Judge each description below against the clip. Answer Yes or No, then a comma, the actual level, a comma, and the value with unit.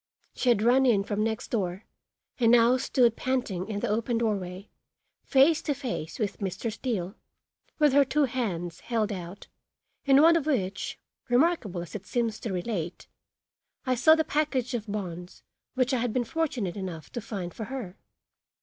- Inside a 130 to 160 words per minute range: No, average, 170 wpm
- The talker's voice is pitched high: Yes, high, 230 Hz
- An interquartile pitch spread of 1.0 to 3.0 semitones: No, average, 5.1 semitones